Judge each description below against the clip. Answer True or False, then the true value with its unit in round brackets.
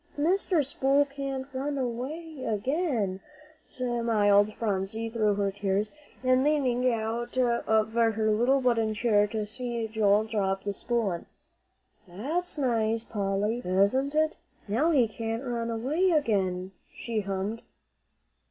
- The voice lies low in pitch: False (230 Hz)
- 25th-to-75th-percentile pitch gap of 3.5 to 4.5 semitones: True (4.1 semitones)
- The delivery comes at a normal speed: False (125 wpm)